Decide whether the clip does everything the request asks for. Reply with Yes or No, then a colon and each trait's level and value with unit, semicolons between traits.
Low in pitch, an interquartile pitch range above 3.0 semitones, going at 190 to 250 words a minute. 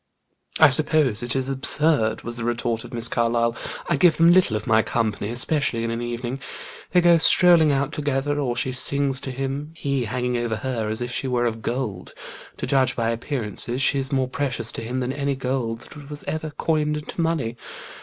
Yes: low, 130 Hz; average, 3.7 semitones; fast, 205 wpm